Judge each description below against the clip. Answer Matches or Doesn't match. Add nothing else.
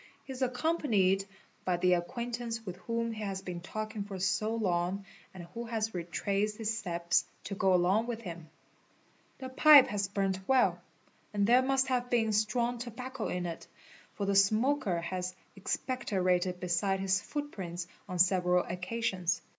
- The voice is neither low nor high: Doesn't match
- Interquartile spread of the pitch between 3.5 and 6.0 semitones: Matches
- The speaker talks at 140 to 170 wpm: Matches